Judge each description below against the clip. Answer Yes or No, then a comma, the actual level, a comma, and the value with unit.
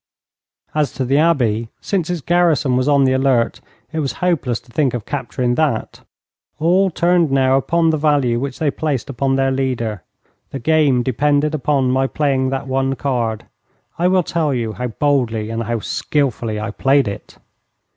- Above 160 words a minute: Yes, average, 175 wpm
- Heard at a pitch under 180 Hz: Yes, low, 135 Hz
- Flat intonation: No, average, 3.7 semitones